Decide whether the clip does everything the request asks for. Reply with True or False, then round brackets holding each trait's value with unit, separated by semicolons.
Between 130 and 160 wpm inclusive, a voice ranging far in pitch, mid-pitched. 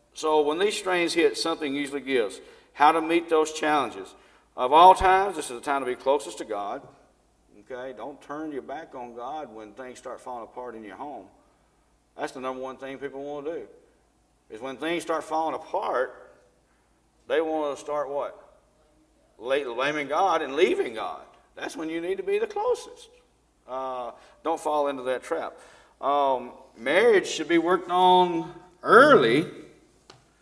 False (170 wpm; 7.4 semitones; 155 Hz)